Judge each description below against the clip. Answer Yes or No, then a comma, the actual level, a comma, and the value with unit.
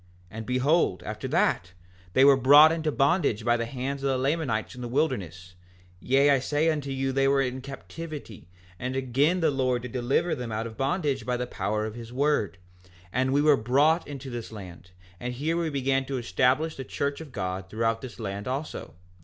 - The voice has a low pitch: Yes, low, 130 Hz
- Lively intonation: No, average, 3.7 semitones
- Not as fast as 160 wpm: No, fast, 205 wpm